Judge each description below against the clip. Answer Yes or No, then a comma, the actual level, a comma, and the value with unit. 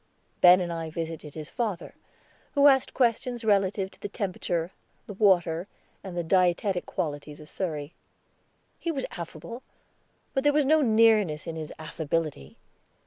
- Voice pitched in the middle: Yes, medium, 180 Hz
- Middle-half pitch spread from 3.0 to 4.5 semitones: No, wide, 5.5 semitones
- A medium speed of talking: Yes, average, 145 wpm